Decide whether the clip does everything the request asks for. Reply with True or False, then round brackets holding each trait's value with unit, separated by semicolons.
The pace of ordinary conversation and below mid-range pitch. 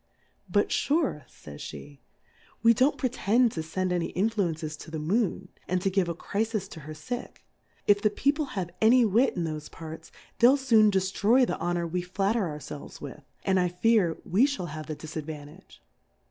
False (180 wpm; 185 Hz)